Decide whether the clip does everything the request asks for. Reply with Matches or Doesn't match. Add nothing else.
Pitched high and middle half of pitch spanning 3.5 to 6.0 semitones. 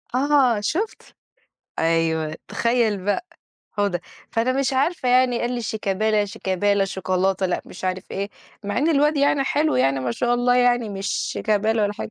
Matches